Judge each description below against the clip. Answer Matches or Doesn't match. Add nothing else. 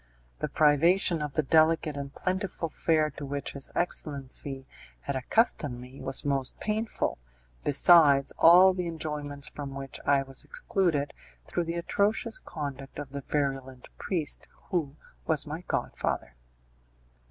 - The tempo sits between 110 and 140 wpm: Matches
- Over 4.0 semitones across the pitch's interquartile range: Doesn't match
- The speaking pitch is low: Doesn't match